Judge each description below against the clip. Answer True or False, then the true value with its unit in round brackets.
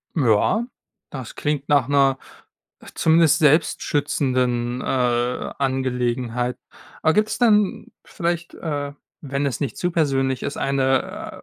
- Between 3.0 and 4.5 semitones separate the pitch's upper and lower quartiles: True (3.7 semitones)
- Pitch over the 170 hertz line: False (135 Hz)